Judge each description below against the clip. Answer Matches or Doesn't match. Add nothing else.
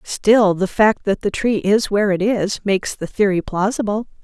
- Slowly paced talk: Doesn't match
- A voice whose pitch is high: Matches